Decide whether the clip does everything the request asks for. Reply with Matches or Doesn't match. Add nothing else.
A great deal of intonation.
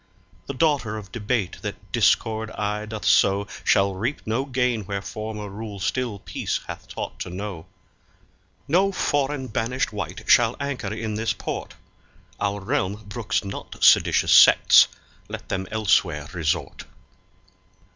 Doesn't match